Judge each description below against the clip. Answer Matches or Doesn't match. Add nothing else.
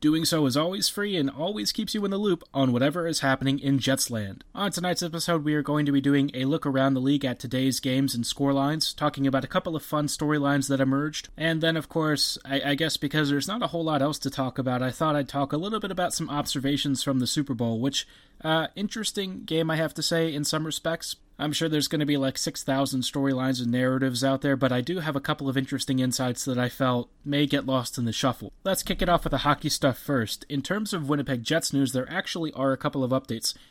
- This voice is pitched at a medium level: Matches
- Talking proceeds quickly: Matches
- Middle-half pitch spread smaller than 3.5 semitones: Matches